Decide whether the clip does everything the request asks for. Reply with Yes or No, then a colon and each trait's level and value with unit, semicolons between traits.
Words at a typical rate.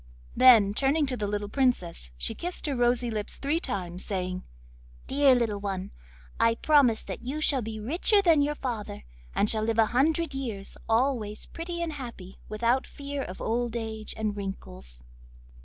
Yes: average, 170 wpm